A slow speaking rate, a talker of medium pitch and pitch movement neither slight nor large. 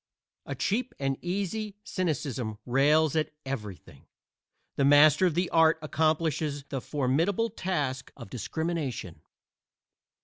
Yes: slow, 110 wpm; medium, 155 Hz; average, 4.4 semitones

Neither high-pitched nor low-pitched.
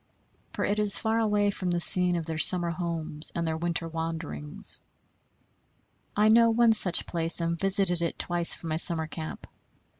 Yes: medium, 170 Hz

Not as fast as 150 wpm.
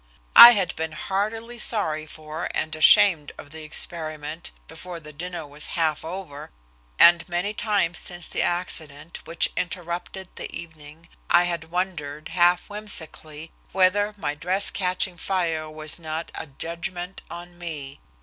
Yes: average, 140 wpm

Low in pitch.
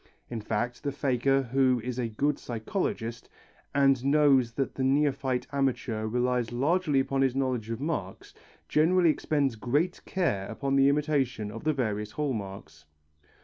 Yes: low, 130 Hz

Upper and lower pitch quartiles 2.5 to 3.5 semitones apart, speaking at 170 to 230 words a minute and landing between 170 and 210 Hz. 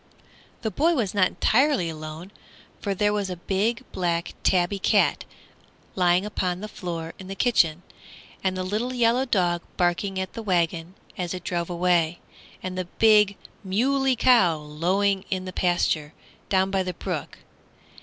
No: average, 3.1 semitones; average, 155 wpm; medium, 185 Hz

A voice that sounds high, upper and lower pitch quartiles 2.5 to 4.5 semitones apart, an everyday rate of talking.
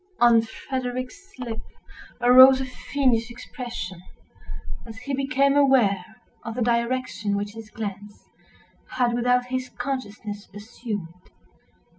No: high, 240 Hz; average, 3.2 semitones; slow, 110 wpm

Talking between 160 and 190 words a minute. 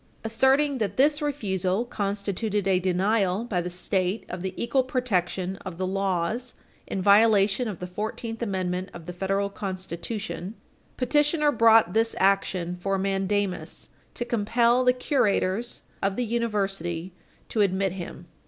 No: average, 140 wpm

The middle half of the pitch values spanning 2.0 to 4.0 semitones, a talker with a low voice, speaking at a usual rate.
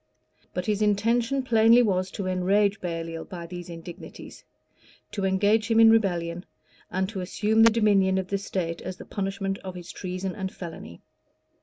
No: average, 2.9 semitones; high, 190 Hz; average, 170 wpm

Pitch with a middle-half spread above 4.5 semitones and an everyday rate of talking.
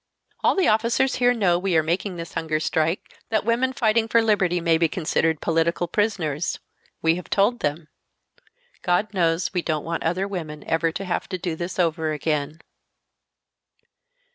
No: average, 4.0 semitones; average, 165 wpm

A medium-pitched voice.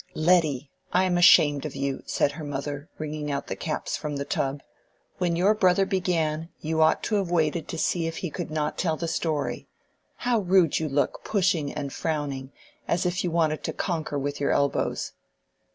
Yes: medium, 155 Hz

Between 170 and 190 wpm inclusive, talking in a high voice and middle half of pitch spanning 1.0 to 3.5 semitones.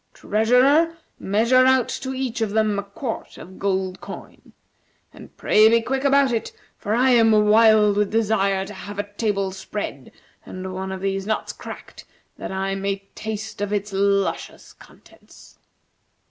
No: average, 160 wpm; high, 210 Hz; narrow, 2.6 semitones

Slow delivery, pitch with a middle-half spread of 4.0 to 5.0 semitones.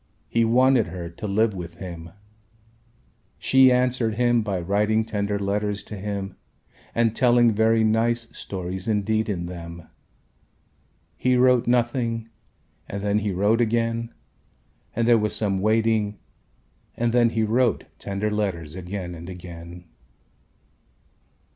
No: slow, 130 wpm; average, 3.3 semitones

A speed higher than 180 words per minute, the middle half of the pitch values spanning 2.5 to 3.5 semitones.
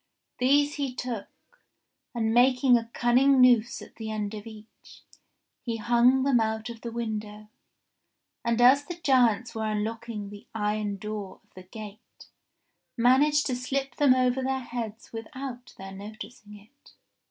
No: average, 150 wpm; average, 3.0 semitones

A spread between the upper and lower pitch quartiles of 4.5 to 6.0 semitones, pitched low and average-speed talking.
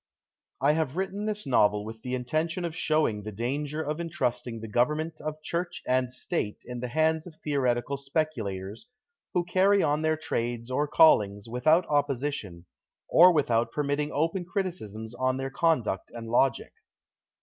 No: average, 5.0 semitones; medium, 145 Hz; average, 160 wpm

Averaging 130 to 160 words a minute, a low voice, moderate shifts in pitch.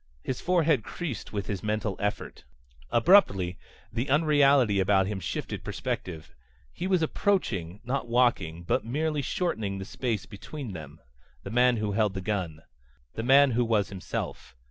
No: average, 150 wpm; low, 110 Hz; wide, 6.2 semitones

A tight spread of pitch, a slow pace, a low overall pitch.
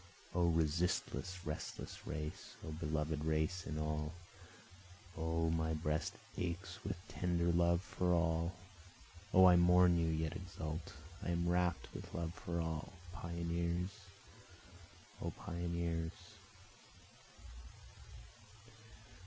Yes: narrow, 1.7 semitones; slow, 105 wpm; very low, 85 Hz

